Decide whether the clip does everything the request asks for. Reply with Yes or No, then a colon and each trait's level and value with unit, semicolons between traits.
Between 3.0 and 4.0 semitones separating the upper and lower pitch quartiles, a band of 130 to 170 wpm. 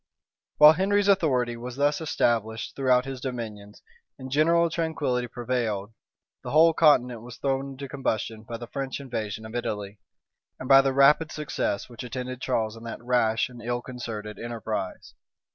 Yes: average, 3.5 semitones; average, 160 wpm